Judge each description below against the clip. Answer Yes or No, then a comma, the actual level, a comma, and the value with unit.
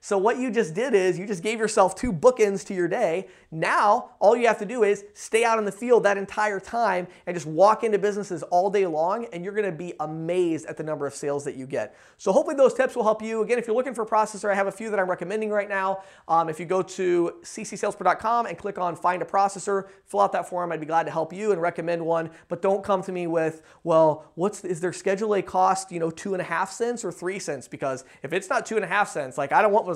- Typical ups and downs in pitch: Yes, average, 3.5 semitones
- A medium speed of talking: No, fast, 270 wpm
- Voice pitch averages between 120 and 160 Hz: No, high, 195 Hz